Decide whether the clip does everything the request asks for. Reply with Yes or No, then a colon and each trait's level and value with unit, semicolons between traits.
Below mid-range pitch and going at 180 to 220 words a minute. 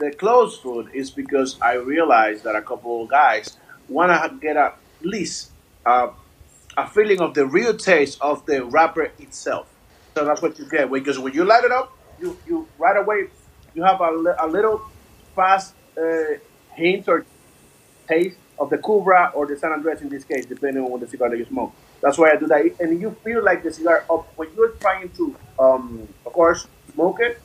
No: medium, 160 Hz; fast, 205 wpm